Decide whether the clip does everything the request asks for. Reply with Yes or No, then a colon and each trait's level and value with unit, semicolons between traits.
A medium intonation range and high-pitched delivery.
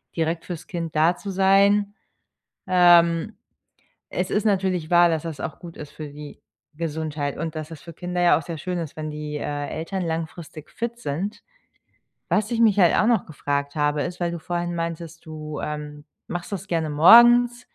No: average, 3.2 semitones; medium, 170 Hz